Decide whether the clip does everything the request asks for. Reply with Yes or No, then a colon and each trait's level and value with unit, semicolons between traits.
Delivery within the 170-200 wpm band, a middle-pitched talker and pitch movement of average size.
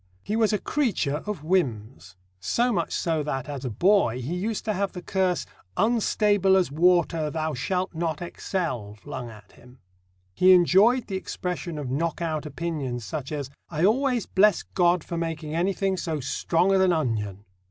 Yes: average, 175 wpm; medium, 170 Hz; average, 5.0 semitones